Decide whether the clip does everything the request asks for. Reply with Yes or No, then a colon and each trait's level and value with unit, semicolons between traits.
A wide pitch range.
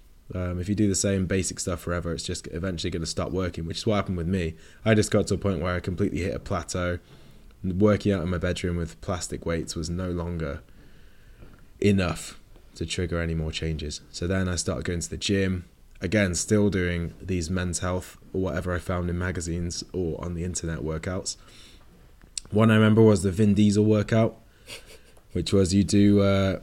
No: average, 2.8 semitones